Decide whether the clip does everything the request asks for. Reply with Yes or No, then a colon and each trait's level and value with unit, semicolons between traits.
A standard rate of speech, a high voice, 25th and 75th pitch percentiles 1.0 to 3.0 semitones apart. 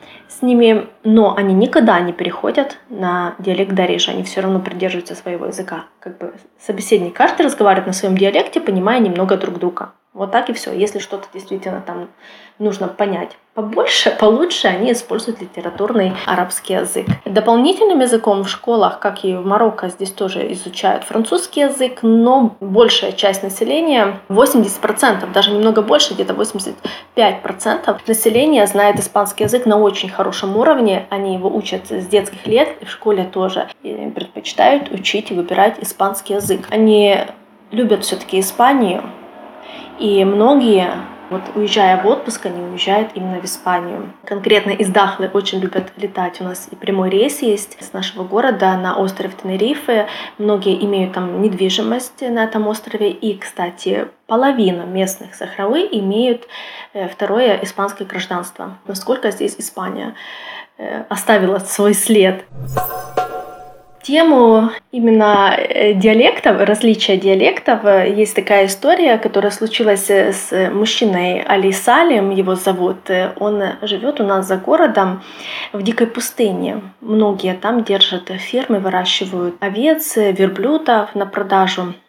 Yes: average, 135 wpm; high, 205 Hz; average, 2.7 semitones